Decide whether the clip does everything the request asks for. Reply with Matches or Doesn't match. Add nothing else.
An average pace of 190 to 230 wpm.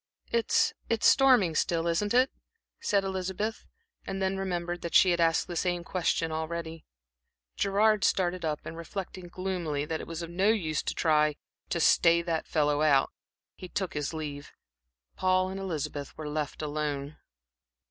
Doesn't match